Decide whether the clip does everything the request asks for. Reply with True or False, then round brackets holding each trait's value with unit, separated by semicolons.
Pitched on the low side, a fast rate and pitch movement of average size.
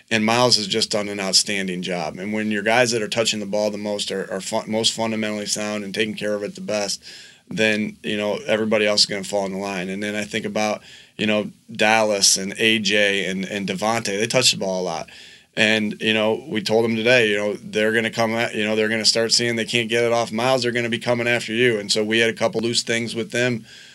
False (110 Hz; 270 wpm; 1.7 semitones)